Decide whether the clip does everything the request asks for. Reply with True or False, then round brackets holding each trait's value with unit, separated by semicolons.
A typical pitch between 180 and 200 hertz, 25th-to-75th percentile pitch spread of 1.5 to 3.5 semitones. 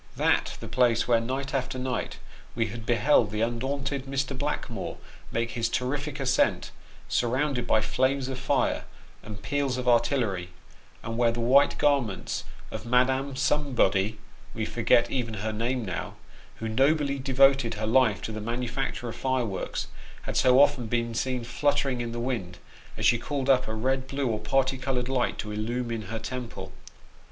False (125 Hz; 2.8 semitones)